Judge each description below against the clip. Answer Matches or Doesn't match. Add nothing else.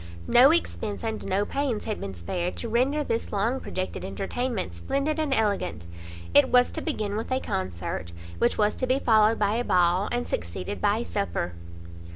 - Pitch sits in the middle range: Doesn't match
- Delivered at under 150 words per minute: Doesn't match